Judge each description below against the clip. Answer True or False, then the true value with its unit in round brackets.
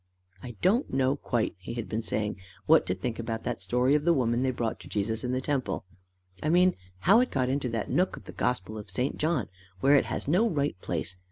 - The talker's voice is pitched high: False (125 Hz)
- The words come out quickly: True (235 wpm)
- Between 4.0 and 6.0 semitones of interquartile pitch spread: True (4.5 semitones)